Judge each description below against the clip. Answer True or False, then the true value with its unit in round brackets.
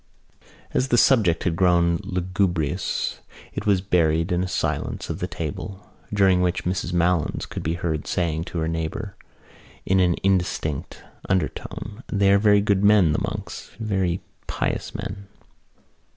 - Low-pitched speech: True (90 Hz)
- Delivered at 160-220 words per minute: False (150 wpm)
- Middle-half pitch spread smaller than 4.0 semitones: True (2.7 semitones)